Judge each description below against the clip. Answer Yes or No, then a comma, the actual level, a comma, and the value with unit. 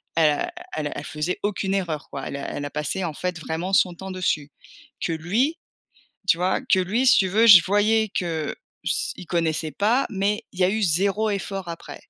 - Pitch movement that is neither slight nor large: Yes, average, 4.1 semitones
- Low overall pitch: No, medium, 185 Hz